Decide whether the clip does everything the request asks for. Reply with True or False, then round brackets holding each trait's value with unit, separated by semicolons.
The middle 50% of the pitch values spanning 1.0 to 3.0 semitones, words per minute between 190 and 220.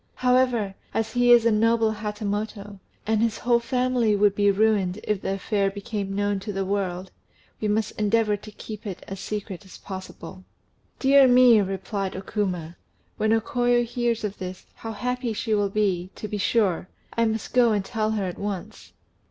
False (2.6 semitones; 180 wpm)